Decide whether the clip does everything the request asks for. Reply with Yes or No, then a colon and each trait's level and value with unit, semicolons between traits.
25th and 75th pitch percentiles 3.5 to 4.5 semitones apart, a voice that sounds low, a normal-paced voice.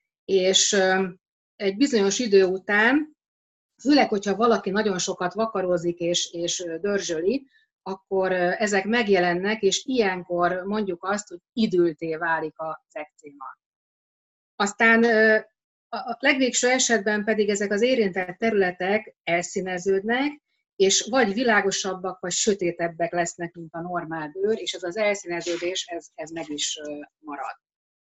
No: average, 3.8 semitones; high, 195 Hz; average, 120 wpm